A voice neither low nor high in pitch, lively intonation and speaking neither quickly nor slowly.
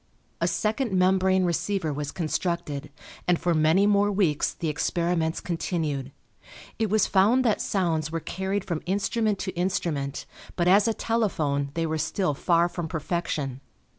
No: medium, 175 Hz; average, 3.7 semitones; average, 150 wpm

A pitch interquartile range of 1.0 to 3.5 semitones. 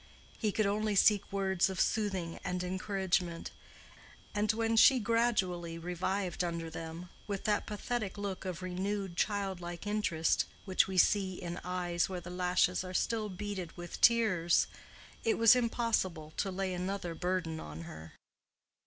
Yes: average, 2.9 semitones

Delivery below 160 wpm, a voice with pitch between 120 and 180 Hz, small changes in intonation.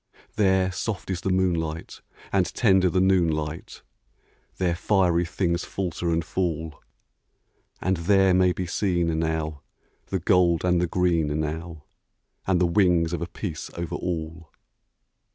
No: average, 140 wpm; very low, 85 Hz; narrow, 2.3 semitones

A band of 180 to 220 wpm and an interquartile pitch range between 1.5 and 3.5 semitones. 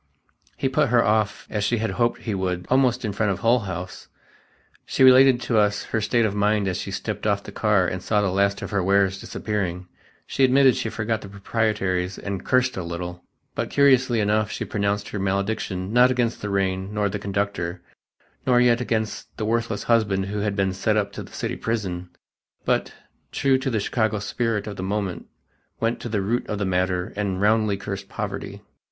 Yes: average, 200 wpm; average, 2.9 semitones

